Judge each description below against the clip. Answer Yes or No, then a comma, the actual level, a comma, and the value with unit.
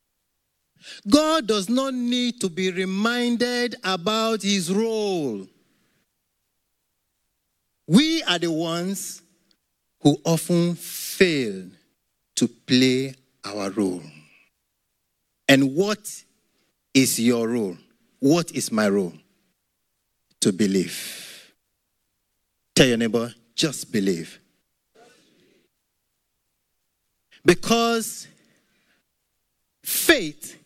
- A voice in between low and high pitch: Yes, medium, 165 Hz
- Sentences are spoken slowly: Yes, slow, 75 wpm